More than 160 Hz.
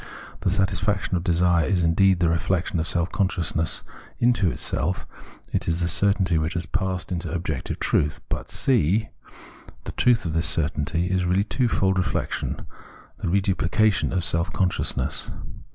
No: very low, 90 Hz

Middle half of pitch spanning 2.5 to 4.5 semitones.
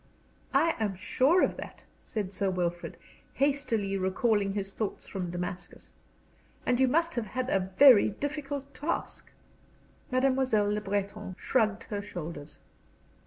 No: average, 5.3 semitones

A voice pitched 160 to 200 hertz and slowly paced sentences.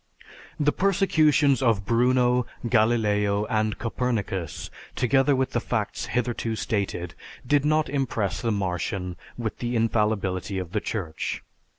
No: low, 115 Hz; slow, 120 wpm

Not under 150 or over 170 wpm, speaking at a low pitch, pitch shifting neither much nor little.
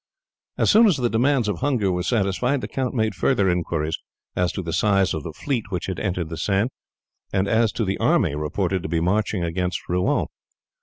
No: fast, 205 wpm; very low, 95 Hz; average, 4.6 semitones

